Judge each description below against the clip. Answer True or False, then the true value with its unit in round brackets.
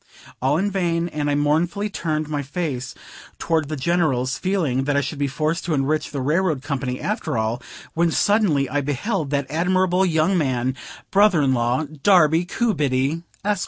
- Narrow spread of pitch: False (4.3 semitones)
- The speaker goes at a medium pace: True (170 wpm)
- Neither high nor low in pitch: True (155 Hz)